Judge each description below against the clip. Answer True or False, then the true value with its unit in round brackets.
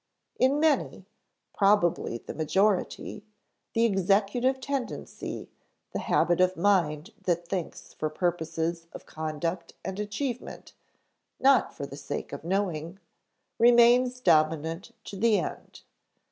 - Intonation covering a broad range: True (5.8 semitones)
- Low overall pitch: False (190 Hz)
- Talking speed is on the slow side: True (115 wpm)